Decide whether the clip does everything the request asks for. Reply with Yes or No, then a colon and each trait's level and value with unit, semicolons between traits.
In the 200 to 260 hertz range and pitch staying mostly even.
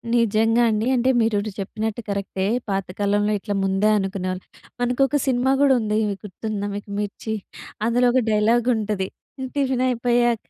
No: high, 220 Hz; average, 3.0 semitones